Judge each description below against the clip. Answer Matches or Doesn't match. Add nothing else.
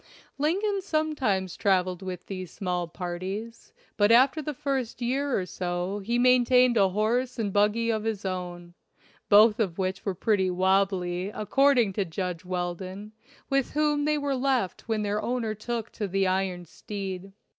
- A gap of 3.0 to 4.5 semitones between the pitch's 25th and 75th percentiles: Doesn't match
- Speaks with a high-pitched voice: Matches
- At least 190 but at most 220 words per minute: Doesn't match